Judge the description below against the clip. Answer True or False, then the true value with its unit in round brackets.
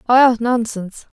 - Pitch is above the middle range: True (235 Hz)